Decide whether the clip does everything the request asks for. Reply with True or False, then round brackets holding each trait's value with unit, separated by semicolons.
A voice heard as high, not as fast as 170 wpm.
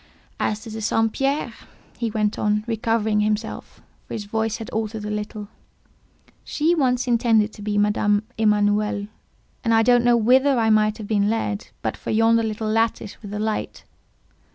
False (220 Hz; 175 wpm)